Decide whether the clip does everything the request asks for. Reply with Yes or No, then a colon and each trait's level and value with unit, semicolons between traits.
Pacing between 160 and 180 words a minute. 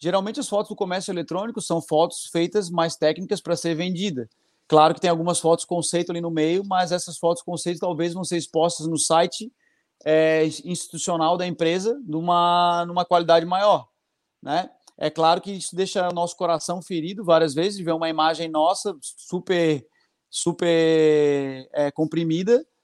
Yes: average, 165 wpm